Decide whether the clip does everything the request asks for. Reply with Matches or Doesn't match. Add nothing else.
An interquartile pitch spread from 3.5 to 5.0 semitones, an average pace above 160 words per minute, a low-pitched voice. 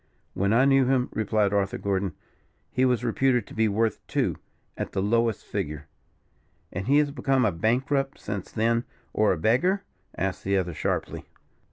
Matches